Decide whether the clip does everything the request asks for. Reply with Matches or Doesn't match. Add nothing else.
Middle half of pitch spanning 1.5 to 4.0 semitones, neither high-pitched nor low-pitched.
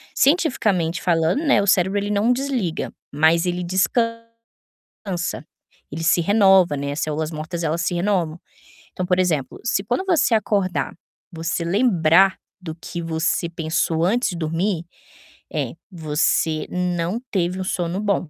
Matches